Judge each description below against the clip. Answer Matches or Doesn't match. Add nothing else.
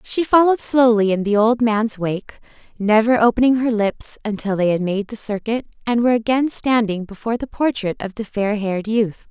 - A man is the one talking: Doesn't match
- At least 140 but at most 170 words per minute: Doesn't match